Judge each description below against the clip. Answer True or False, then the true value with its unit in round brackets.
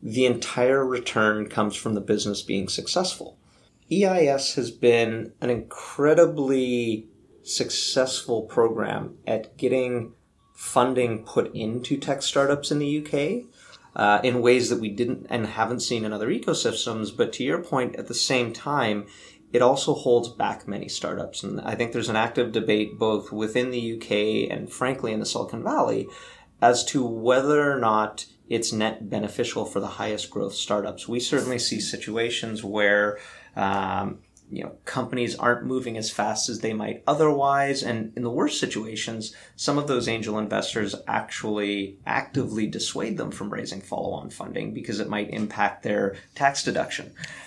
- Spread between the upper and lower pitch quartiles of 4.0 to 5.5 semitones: False (2.9 semitones)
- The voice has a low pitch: True (115 Hz)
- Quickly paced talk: False (155 wpm)